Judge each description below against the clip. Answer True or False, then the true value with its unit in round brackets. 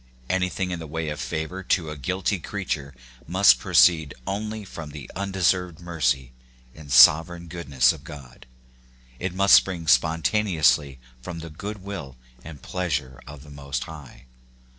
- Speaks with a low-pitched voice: True (80 Hz)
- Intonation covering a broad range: False (4.3 semitones)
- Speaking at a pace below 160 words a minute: True (145 wpm)